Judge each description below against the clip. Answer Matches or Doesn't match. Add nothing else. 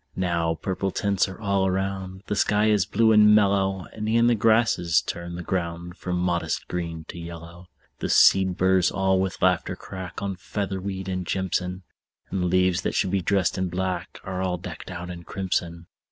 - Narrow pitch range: Matches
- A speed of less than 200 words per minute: Matches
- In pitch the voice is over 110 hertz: Doesn't match